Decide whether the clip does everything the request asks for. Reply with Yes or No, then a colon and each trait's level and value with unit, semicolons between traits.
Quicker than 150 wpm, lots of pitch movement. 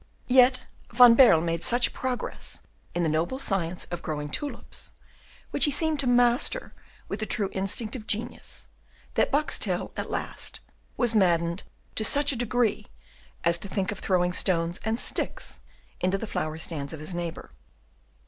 Yes: average, 160 wpm; wide, 6.3 semitones